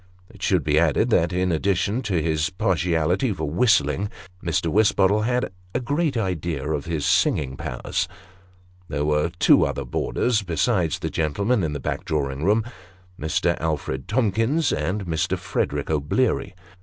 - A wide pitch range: Yes, wide, 5.7 semitones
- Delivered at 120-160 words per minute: Yes, average, 150 wpm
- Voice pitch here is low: Yes, very low, 85 Hz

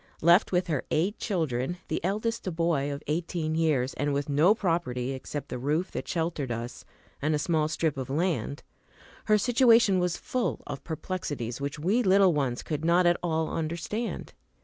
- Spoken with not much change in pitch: No, average, 4.2 semitones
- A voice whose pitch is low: No, medium, 160 Hz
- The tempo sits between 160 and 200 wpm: Yes, average, 175 wpm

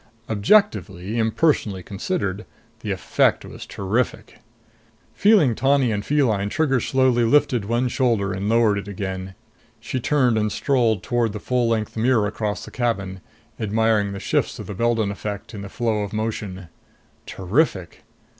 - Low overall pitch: Yes, low, 110 Hz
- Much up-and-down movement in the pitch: No, average, 3.5 semitones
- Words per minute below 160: Yes, average, 145 wpm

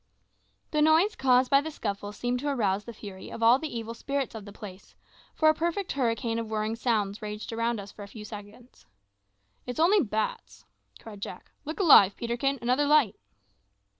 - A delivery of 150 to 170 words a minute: No, average, 185 wpm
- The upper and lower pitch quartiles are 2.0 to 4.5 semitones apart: No, average, 4.9 semitones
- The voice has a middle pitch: No, high, 235 Hz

